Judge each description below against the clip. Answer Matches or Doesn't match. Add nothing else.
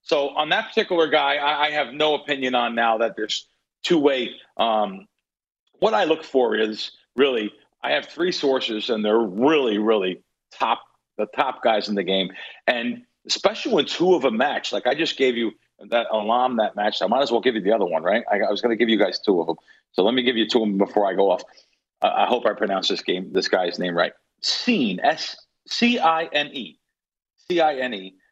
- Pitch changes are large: Matches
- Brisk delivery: Matches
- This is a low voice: Matches